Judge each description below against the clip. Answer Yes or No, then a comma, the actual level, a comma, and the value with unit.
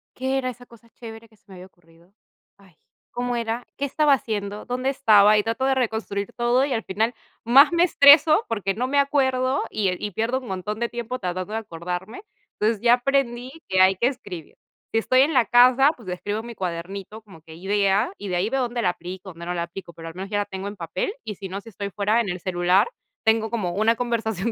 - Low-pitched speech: No, high, 220 Hz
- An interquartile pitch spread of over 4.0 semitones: Yes, average, 4.6 semitones